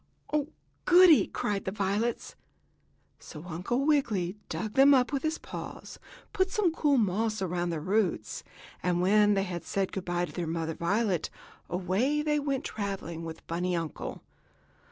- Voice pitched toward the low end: No, high, 200 Hz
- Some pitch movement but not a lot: No, wide, 7.3 semitones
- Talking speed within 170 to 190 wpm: No, average, 160 wpm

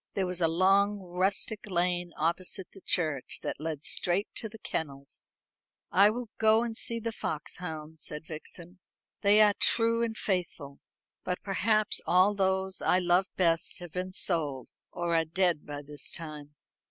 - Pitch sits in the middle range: Yes, medium, 180 Hz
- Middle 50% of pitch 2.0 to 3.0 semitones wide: No, average, 3.8 semitones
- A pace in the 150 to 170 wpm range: Yes, average, 160 wpm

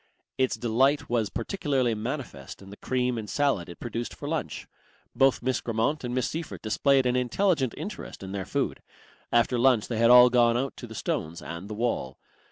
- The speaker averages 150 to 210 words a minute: Yes, average, 190 wpm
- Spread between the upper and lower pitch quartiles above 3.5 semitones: No, average, 3.0 semitones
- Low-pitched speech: Yes, low, 120 Hz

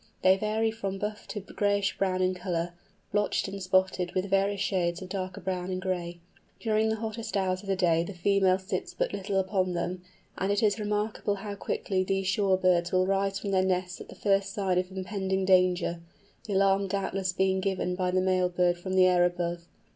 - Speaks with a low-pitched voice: No, high, 190 Hz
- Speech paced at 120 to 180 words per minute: No, average, 200 wpm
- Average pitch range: No, narrow, 1.5 semitones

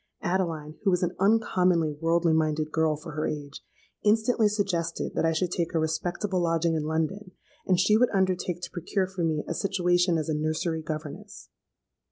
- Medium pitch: Yes, medium, 170 Hz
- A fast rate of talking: No, average, 180 wpm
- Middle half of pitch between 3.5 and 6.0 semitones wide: No, average, 2.9 semitones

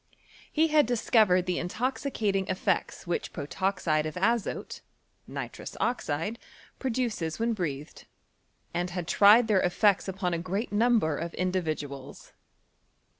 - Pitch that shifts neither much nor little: Yes, average, 4.8 semitones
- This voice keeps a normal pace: No, slow, 120 wpm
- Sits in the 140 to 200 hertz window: Yes, high, 190 Hz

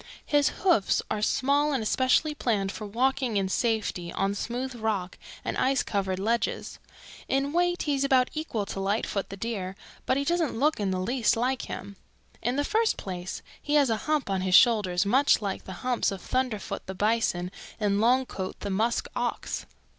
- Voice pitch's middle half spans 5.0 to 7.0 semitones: Yes, average, 5.3 semitones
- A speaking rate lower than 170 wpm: No, average, 185 wpm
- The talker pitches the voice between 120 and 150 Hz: No, high, 225 Hz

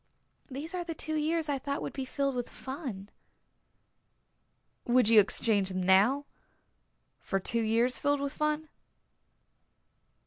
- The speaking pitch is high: Yes, very high, 265 Hz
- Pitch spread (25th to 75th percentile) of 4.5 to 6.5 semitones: Yes, average, 5.2 semitones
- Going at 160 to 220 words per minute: No, slow, 135 wpm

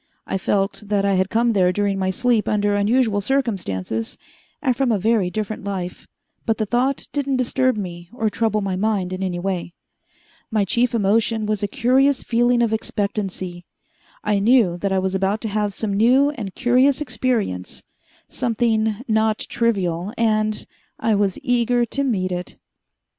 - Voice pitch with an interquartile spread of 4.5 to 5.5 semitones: No, average, 3.7 semitones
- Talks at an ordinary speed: Yes, average, 165 wpm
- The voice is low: No, high, 215 Hz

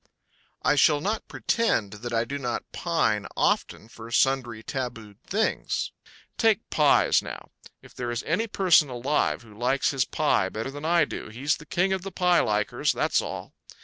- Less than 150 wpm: No, average, 175 wpm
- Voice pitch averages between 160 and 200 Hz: No, low, 135 Hz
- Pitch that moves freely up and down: Yes, wide, 6.6 semitones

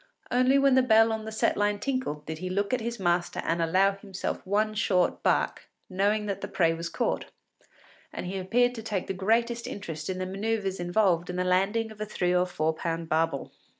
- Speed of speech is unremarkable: No, fast, 215 wpm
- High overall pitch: Yes, high, 195 Hz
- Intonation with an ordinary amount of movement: Yes, average, 3.7 semitones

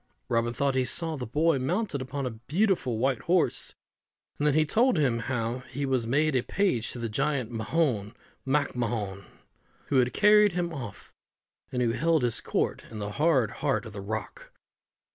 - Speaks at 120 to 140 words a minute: No, average, 180 wpm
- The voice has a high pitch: No, low, 130 Hz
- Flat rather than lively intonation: No, average, 4.9 semitones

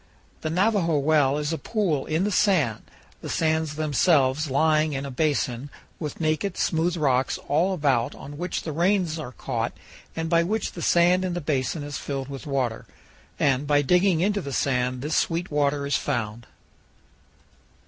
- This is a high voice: No, medium, 150 Hz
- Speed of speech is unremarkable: Yes, average, 170 wpm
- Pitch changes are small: No, average, 3.6 semitones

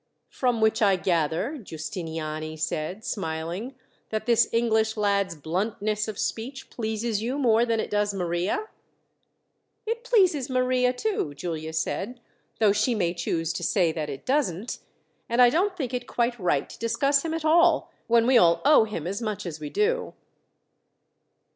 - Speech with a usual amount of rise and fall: No, wide, 6.6 semitones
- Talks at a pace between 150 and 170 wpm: Yes, average, 160 wpm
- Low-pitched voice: No, high, 220 Hz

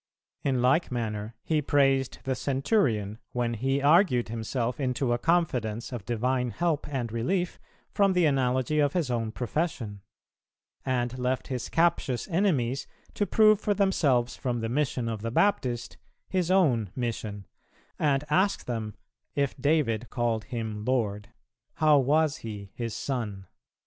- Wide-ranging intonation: No, average, 4.5 semitones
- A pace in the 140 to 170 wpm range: Yes, average, 145 wpm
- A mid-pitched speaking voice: No, low, 125 Hz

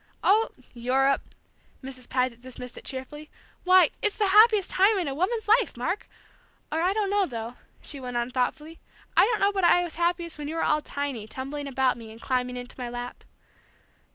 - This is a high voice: Yes, very high, 290 Hz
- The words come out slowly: No, average, 200 wpm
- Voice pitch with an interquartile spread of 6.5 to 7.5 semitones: Yes, wide, 6.8 semitones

